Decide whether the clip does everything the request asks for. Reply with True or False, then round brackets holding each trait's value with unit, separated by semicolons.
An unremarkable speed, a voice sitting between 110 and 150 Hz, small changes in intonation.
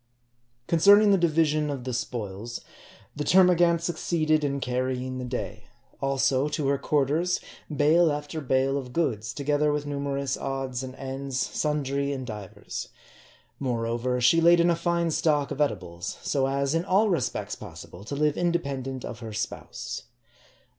False (155 wpm; 140 Hz; 3.7 semitones)